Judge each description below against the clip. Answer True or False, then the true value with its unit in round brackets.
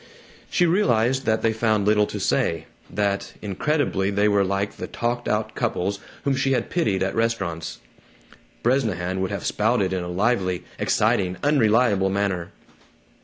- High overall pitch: False (105 Hz)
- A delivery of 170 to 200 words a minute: False (150 wpm)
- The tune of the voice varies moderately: True (3.7 semitones)